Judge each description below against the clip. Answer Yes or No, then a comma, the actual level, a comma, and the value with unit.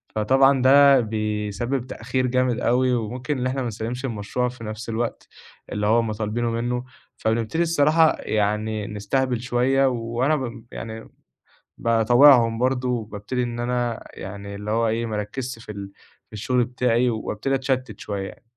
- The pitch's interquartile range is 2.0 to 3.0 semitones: Yes, average, 2.7 semitones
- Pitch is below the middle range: Yes, low, 120 Hz